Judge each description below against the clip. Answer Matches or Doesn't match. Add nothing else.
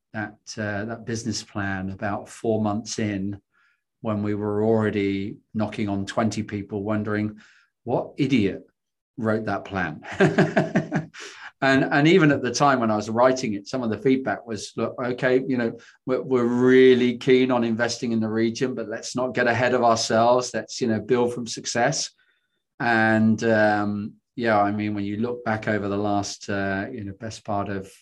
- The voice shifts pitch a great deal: Doesn't match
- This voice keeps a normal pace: Matches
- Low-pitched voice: Matches